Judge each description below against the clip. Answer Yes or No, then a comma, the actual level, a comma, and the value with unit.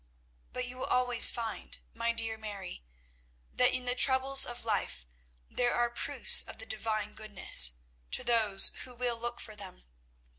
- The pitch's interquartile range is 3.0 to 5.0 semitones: No, narrow, 2.6 semitones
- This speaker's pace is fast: No, average, 160 wpm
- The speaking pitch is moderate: No, high, 230 Hz